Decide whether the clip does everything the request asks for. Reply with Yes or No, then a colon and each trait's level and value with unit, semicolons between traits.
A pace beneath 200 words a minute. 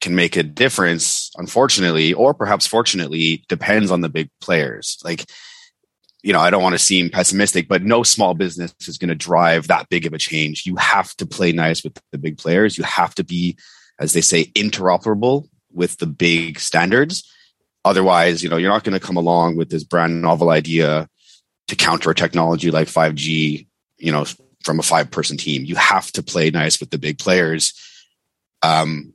Yes: average, 190 wpm